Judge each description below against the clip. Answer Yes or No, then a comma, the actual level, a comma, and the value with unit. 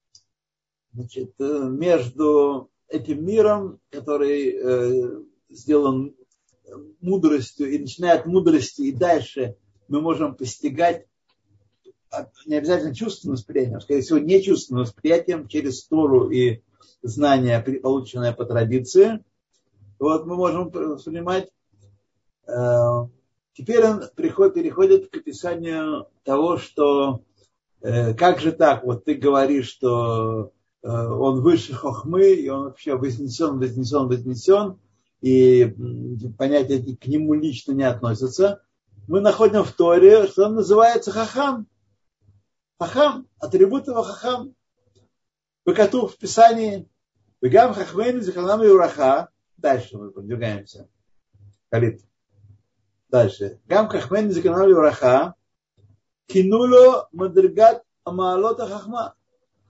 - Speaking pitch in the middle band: Yes, medium, 145 Hz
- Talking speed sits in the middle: No, slow, 105 wpm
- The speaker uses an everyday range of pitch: No, wide, 8.0 semitones